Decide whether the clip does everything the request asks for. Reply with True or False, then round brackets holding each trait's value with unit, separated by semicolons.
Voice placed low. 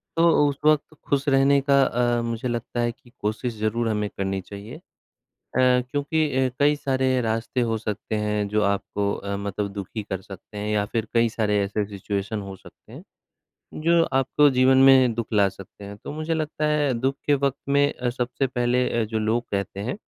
True (120 Hz)